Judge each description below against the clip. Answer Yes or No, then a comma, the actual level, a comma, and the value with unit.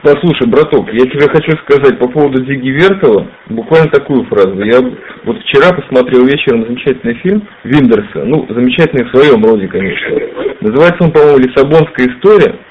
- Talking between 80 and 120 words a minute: No, average, 155 wpm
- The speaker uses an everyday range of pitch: No, wide, 7.2 semitones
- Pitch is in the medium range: Yes, medium, 145 Hz